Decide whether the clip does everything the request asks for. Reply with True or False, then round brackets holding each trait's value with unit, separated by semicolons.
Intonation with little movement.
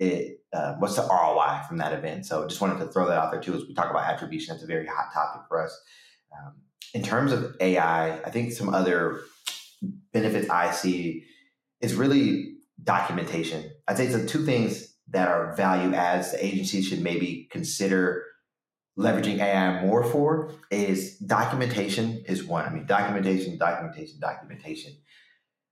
False (4.4 semitones)